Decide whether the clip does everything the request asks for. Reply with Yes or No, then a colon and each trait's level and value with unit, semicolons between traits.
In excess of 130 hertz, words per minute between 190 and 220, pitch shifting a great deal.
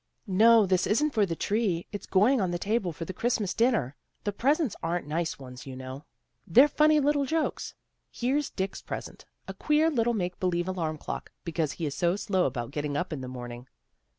Yes: medium, 185 Hz; average, 200 wpm; wide, 7.1 semitones